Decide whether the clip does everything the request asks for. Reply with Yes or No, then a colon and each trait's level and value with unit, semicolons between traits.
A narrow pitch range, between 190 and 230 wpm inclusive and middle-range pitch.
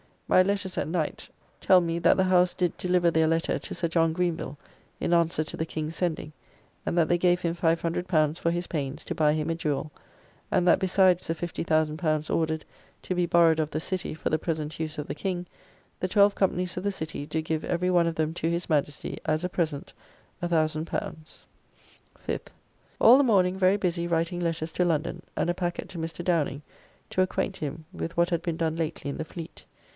Yes: narrow, 2.2 semitones; fast, 205 wpm; medium, 170 Hz